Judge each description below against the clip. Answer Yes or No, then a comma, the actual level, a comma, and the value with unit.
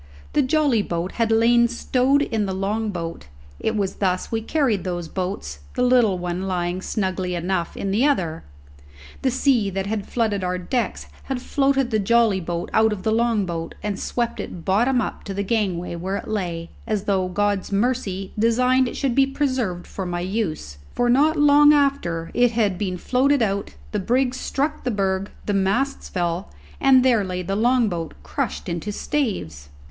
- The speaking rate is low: No, average, 185 wpm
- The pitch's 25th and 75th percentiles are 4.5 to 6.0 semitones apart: Yes, average, 5.2 semitones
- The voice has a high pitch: Yes, high, 205 Hz